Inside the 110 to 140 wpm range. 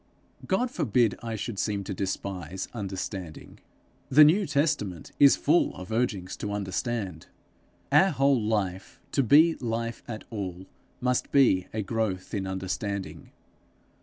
Yes: slow, 135 wpm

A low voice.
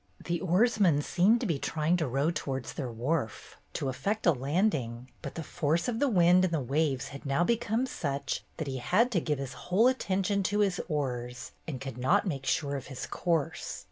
No: medium, 160 Hz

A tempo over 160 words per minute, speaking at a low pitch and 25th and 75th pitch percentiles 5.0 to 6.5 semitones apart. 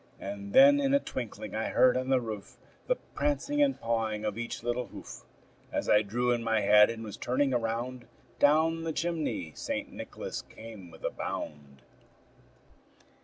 Yes: average, 170 wpm; low, 115 Hz; average, 5.3 semitones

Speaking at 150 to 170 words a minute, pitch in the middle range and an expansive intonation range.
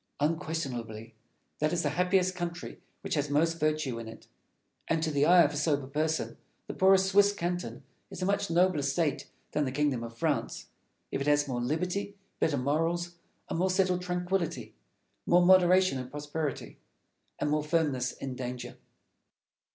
No: average, 160 wpm; medium, 160 Hz; average, 4.1 semitones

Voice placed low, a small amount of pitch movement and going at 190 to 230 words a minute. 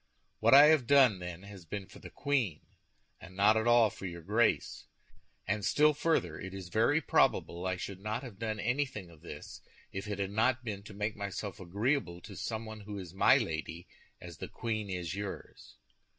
No: low, 105 Hz; average, 3.9 semitones; average, 195 wpm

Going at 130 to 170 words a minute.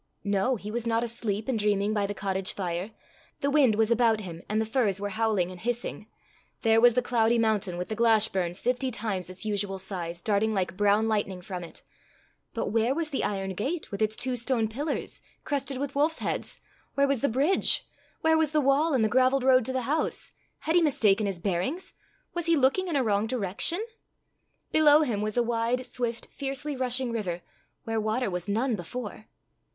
No: average, 200 wpm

